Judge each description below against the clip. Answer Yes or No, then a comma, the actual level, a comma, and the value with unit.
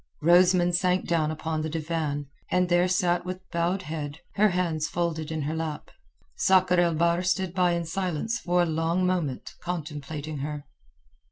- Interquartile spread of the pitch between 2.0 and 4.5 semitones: Yes, narrow, 2.5 semitones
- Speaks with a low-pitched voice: No, medium, 170 Hz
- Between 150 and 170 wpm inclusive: Yes, average, 165 wpm